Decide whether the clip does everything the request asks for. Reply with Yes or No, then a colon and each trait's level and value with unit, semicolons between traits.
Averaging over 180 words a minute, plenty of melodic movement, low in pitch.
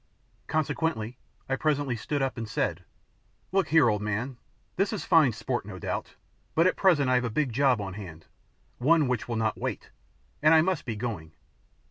Yes: average, 190 wpm; wide, 5.9 semitones; low, 130 Hz